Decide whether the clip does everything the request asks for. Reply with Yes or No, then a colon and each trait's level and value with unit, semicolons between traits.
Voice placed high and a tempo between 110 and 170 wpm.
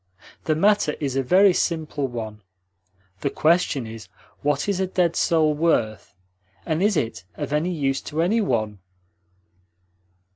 No: medium, 155 Hz; average, 145 wpm